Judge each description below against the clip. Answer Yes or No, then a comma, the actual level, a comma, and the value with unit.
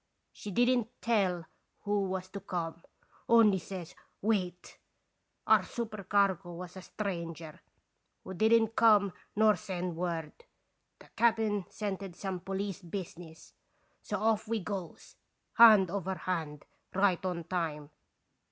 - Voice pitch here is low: No, high, 190 Hz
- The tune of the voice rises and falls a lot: No, average, 3.1 semitones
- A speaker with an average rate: No, slow, 120 wpm